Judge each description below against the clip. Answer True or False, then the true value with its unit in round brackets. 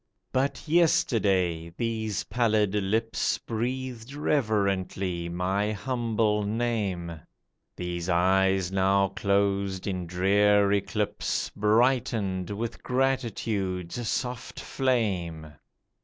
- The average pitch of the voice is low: True (100 Hz)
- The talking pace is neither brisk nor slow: False (80 wpm)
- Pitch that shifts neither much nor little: True (3.6 semitones)